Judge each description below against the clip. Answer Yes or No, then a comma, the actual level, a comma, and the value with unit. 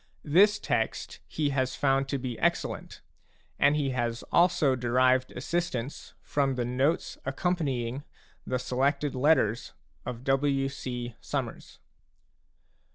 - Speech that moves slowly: Yes, slow, 115 wpm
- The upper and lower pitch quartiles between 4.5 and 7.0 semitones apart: No, narrow, 2.5 semitones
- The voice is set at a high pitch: No, low, 135 Hz